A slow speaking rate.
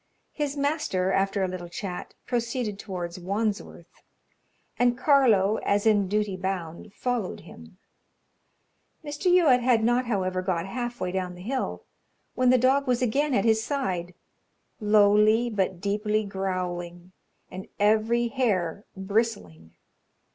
Yes: slow, 130 wpm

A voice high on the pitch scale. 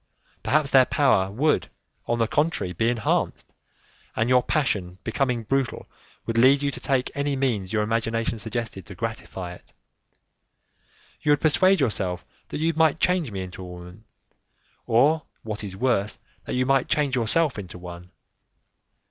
No: low, 115 Hz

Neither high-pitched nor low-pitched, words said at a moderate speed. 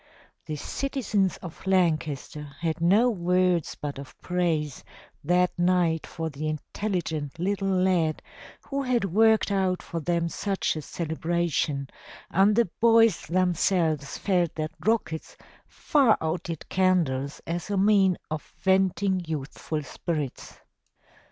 No: medium, 175 Hz; slow, 120 wpm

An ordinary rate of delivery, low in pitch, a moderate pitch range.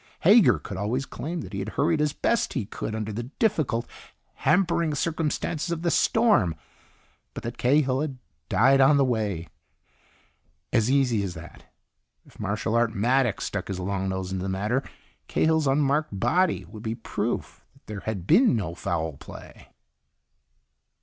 No: average, 160 wpm; low, 120 Hz; wide, 7.0 semitones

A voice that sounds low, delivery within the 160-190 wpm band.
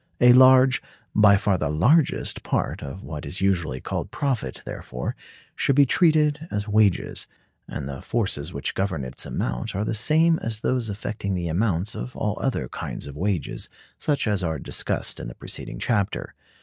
Yes: low, 105 Hz; average, 165 wpm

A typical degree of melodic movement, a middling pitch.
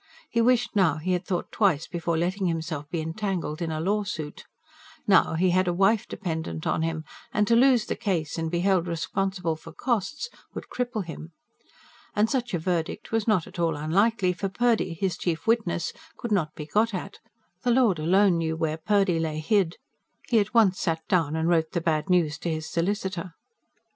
Yes: average, 4.1 semitones; medium, 180 Hz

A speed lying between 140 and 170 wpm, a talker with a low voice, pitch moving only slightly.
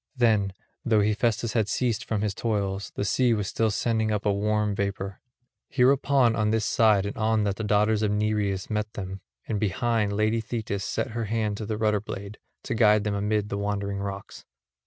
No: average, 195 wpm; low, 105 Hz; narrow, 1.6 semitones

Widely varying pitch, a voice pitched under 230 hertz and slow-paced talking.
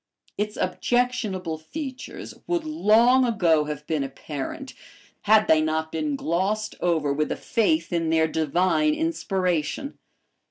Yes: wide, 7.6 semitones; medium, 185 Hz; slow, 125 wpm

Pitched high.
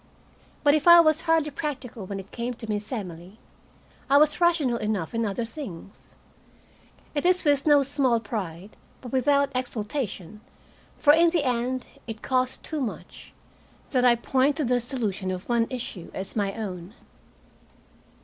Yes: high, 245 Hz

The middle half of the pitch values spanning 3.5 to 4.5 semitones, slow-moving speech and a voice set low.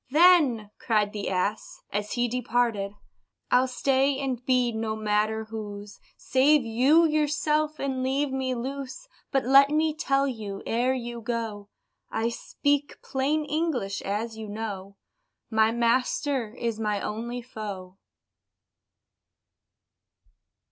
No: average, 4.0 semitones; slow, 120 wpm; high, 240 Hz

